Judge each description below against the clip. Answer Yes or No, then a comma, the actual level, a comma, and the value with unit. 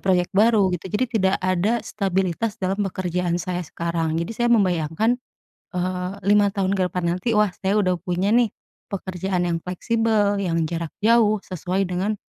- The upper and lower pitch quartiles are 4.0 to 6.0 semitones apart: No, average, 2.7 semitones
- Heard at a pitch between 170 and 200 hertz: Yes, medium, 185 Hz